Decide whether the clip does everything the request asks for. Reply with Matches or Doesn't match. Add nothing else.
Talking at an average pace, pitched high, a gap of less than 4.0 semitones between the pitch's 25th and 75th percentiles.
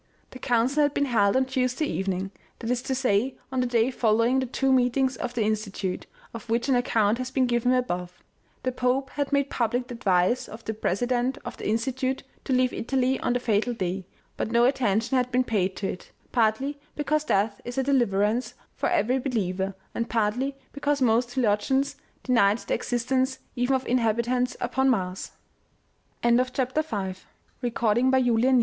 Matches